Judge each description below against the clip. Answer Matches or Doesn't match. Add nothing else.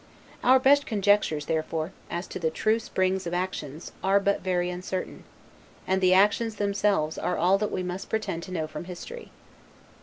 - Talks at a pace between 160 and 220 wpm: Matches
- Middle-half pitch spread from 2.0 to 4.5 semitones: Matches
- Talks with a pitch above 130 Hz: Matches